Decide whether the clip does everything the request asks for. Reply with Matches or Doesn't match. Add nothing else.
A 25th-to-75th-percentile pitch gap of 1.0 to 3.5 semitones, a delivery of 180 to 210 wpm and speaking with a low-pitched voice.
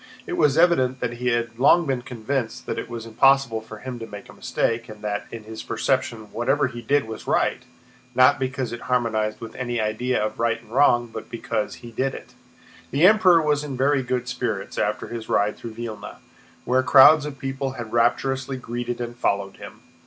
Matches